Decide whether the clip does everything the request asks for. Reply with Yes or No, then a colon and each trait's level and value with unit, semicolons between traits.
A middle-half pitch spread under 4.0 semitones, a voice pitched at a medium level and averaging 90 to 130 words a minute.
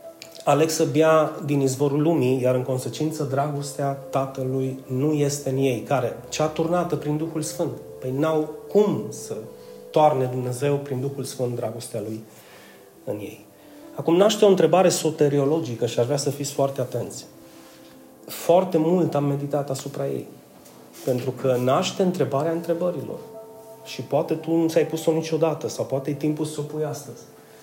No: average, 3.5 semitones; medium, 145 Hz; average, 155 wpm